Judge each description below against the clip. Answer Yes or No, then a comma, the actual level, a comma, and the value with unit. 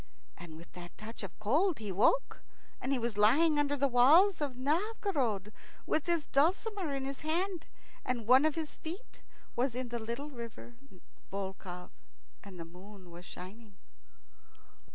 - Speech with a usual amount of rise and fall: No, wide, 7.1 semitones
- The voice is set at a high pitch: Yes, very high, 250 Hz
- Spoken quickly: No, average, 155 wpm